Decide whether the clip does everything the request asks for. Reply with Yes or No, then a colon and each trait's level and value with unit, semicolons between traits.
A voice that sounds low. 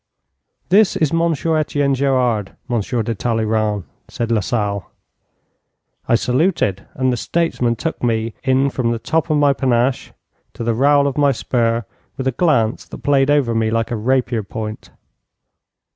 Yes: low, 125 Hz